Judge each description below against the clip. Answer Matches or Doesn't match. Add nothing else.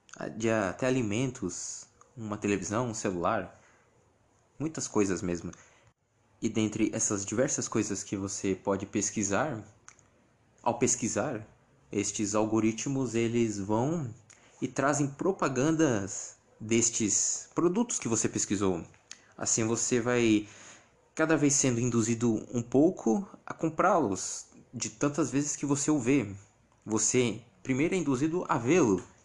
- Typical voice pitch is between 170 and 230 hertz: Doesn't match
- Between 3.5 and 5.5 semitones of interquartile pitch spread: Matches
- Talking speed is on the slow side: Matches